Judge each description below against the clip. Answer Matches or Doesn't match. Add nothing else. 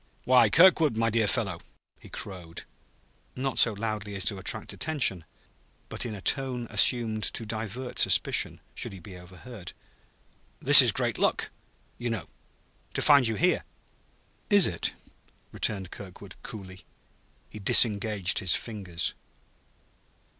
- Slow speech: Matches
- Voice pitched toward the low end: Matches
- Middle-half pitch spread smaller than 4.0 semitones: Doesn't match